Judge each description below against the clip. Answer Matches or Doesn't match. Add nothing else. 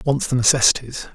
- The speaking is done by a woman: Doesn't match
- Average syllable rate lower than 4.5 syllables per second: Doesn't match